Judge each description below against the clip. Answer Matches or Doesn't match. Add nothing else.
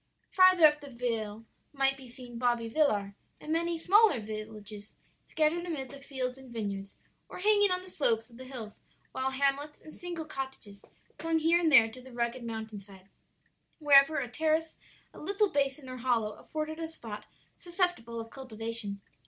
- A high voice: Matches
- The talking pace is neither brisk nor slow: Matches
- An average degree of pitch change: Doesn't match